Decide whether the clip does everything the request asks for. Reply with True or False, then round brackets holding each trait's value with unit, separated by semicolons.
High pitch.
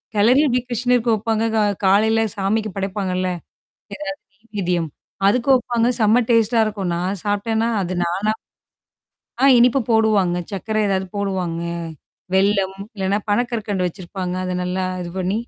True (205 Hz)